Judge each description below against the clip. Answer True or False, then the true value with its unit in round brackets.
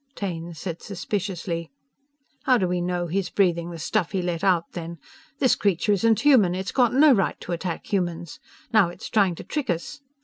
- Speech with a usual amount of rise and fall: True (3.2 semitones)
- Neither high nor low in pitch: True (180 Hz)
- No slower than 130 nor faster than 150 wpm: False (190 wpm)